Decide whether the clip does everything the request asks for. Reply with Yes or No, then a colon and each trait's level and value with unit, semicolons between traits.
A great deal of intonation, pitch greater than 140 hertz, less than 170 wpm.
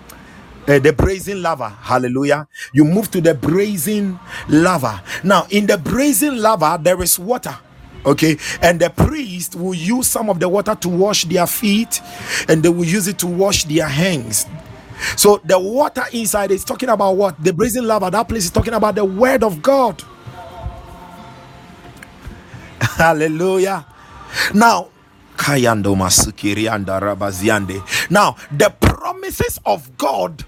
Yes: wide, 5.8 semitones; medium, 185 Hz; slow, 135 wpm